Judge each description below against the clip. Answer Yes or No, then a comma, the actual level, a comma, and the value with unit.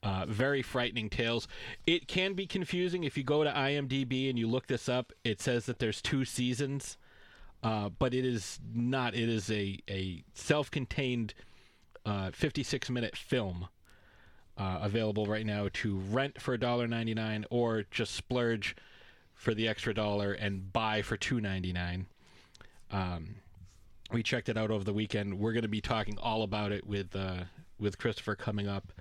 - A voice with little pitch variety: No, average, 3.8 semitones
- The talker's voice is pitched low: Yes, low, 110 Hz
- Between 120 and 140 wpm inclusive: No, average, 170 wpm